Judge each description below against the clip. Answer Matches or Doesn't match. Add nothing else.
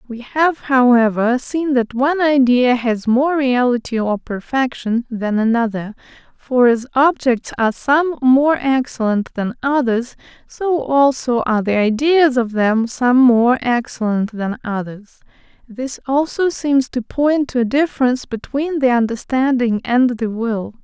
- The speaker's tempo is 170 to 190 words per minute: Doesn't match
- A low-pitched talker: Doesn't match